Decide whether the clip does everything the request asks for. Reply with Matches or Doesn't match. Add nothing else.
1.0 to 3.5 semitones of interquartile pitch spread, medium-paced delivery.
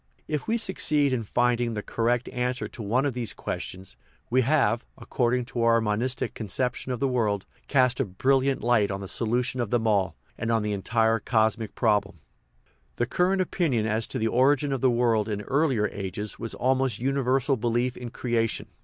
Matches